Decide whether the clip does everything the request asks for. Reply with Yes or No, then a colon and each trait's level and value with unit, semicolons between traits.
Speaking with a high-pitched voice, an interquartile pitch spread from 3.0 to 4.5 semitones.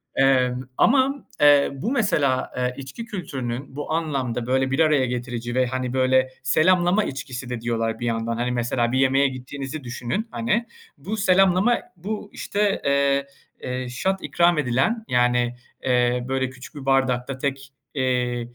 No: low, 130 Hz; average, 4.1 semitones